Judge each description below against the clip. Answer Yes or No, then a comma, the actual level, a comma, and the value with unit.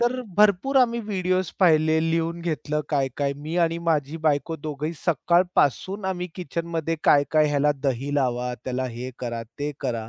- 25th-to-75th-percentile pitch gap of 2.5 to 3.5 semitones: No, average, 3.9 semitones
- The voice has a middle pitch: Yes, medium, 155 Hz